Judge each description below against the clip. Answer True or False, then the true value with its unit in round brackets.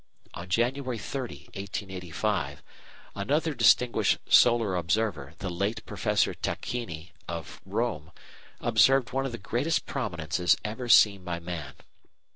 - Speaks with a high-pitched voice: False (105 Hz)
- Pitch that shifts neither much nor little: False (5.7 semitones)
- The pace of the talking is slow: True (115 wpm)